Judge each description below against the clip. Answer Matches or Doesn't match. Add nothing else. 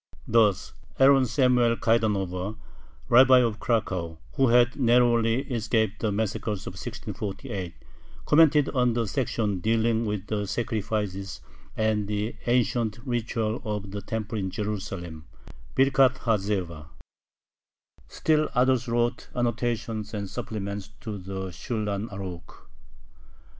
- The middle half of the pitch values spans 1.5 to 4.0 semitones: Matches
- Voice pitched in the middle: Doesn't match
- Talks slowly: Matches